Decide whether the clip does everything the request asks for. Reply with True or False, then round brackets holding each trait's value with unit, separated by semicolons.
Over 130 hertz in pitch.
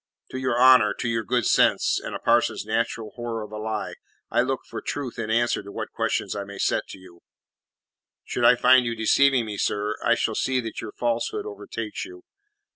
False (115 Hz)